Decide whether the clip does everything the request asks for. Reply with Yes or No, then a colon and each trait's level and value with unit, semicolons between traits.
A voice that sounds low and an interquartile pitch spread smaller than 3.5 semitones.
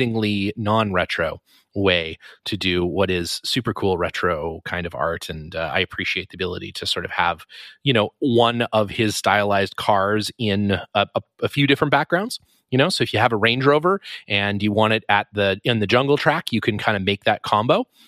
Yes: low, 105 Hz; average, 3.0 semitones